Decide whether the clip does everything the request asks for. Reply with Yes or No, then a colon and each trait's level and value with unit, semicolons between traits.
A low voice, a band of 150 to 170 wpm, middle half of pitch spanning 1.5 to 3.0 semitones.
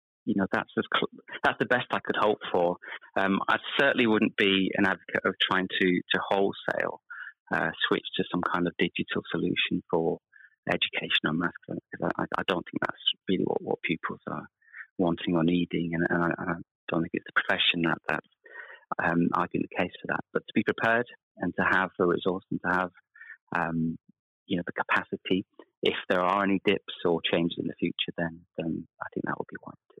No: very low, 85 Hz; fast, 205 wpm; narrow, 2.5 semitones